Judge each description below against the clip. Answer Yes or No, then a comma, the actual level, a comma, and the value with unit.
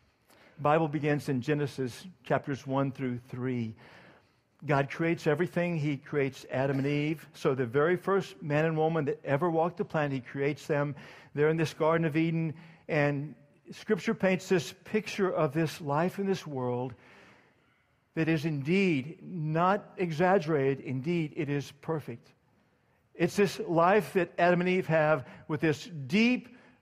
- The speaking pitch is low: No, medium, 160 Hz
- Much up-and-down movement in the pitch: No, average, 3.7 semitones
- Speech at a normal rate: Yes, average, 150 wpm